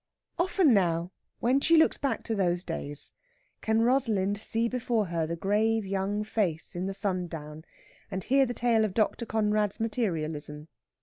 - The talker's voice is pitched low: No, high, 205 Hz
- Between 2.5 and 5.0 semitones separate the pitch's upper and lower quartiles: Yes, average, 4.7 semitones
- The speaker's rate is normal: Yes, average, 160 wpm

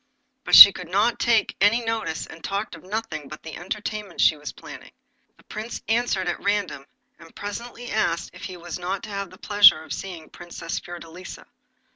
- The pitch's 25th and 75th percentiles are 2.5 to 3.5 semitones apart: No, average, 3.9 semitones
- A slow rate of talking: No, average, 190 wpm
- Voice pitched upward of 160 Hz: Yes, high, 190 Hz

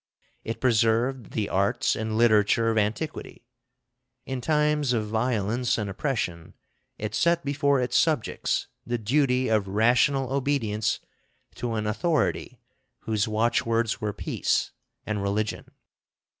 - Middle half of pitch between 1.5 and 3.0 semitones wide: No, average, 3.7 semitones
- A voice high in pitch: No, low, 115 Hz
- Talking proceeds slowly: Yes, slow, 120 wpm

